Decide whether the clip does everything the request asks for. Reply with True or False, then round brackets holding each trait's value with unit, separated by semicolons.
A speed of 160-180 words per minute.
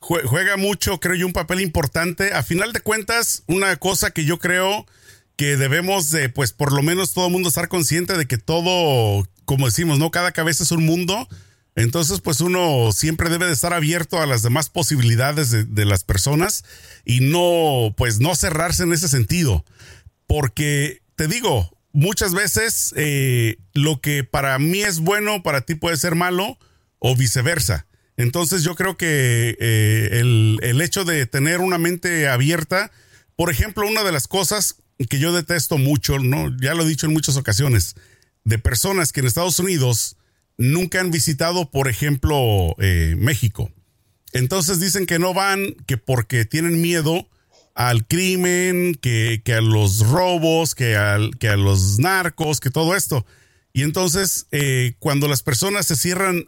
True (170 wpm)